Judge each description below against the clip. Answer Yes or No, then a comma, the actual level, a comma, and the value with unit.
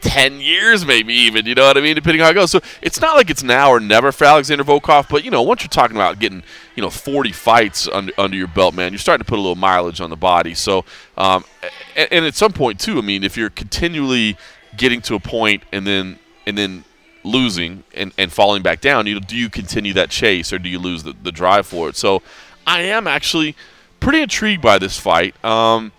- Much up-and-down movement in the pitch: Yes, wide, 6.7 semitones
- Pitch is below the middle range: Yes, low, 115 Hz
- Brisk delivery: Yes, fast, 240 wpm